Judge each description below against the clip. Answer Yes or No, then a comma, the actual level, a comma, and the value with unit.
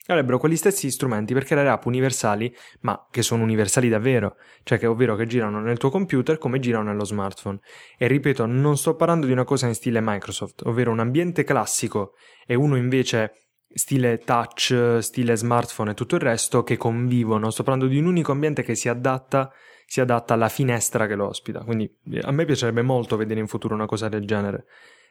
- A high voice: No, low, 120 Hz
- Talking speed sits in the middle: No, fast, 195 wpm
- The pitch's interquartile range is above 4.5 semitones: No, average, 3.1 semitones